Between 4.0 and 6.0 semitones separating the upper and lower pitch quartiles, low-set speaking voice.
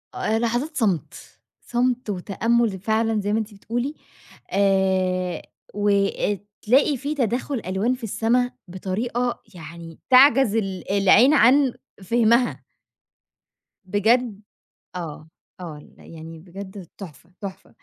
No: average, 4.3 semitones; high, 210 Hz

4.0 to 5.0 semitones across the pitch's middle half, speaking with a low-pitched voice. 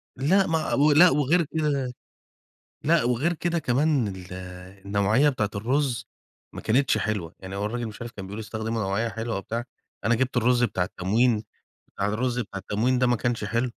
Yes: average, 4.6 semitones; low, 120 Hz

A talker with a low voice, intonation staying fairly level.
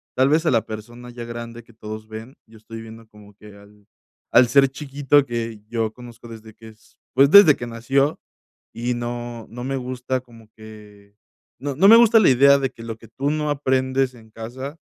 No: low, 120 Hz; average, 3.3 semitones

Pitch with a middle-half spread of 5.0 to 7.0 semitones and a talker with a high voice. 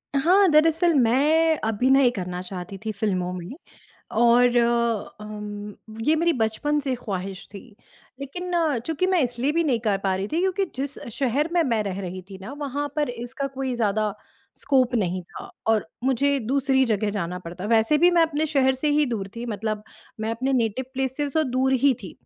Yes: wide, 5.5 semitones; very high, 250 Hz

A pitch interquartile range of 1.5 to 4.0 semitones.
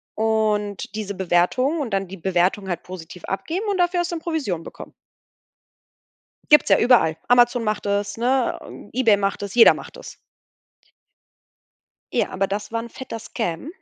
No: average, 4.7 semitones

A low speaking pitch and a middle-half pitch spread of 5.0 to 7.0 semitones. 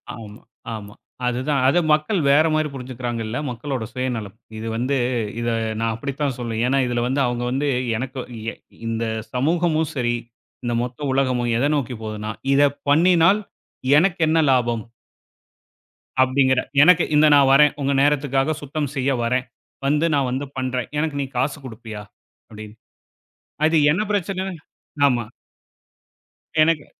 No: low, 130 Hz; average, 3.7 semitones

